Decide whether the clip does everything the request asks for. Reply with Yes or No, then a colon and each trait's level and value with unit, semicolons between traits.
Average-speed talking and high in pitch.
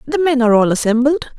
No: fast, 215 wpm; very high, 260 Hz